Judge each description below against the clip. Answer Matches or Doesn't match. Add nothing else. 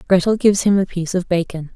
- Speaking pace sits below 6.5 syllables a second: Doesn't match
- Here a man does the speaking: Doesn't match